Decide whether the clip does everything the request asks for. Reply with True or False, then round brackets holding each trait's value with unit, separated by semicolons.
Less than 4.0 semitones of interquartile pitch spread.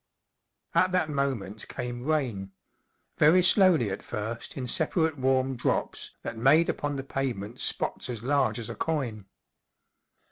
False (4.7 semitones)